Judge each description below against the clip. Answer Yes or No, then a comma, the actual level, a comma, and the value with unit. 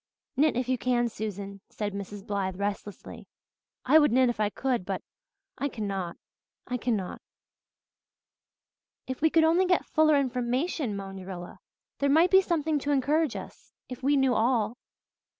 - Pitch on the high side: Yes, very high, 250 Hz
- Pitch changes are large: Yes, wide, 6.1 semitones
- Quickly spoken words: No, average, 155 wpm